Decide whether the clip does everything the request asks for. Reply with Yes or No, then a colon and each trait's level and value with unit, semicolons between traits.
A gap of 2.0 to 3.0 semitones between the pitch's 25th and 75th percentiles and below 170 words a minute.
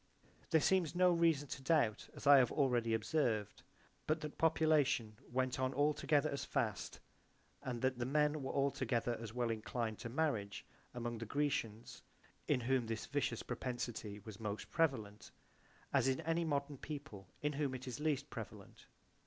No: average, 4.4 semitones; average, 160 wpm